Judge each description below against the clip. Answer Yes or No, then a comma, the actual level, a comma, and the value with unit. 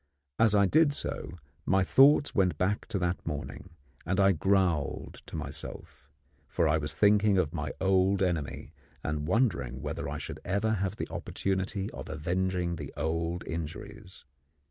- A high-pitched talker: No, very low, 95 Hz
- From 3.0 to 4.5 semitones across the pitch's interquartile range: Yes, average, 3.6 semitones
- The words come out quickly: No, average, 155 wpm